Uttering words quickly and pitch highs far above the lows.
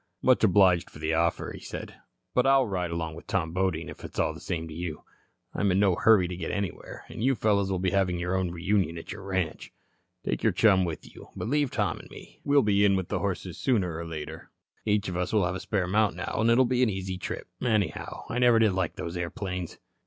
No: fast, 240 wpm; average, 3.5 semitones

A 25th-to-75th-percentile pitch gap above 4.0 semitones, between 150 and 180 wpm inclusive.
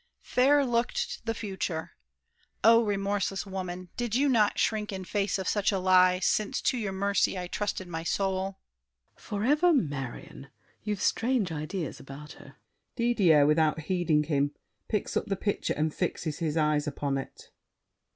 Yes: average, 4.8 semitones; average, 155 wpm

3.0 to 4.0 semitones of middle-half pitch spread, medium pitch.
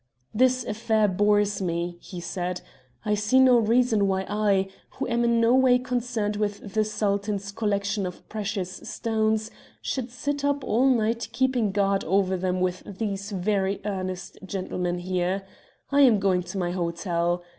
No: average, 3.5 semitones; high, 205 Hz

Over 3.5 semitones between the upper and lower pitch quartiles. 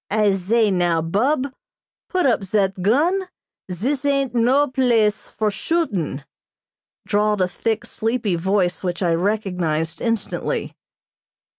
Yes: wide, 5.6 semitones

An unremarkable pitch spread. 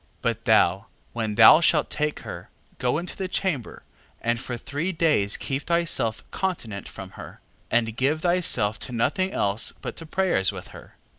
No: wide, 7.1 semitones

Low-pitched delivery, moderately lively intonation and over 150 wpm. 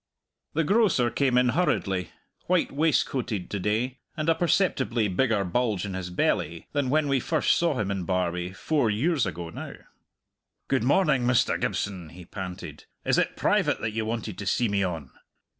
No: low, 115 Hz; wide, 6.9 semitones; average, 175 wpm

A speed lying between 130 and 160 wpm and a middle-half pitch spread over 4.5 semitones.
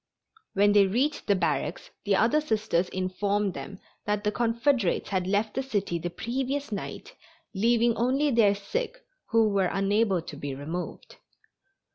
No: average, 150 wpm; average, 3.8 semitones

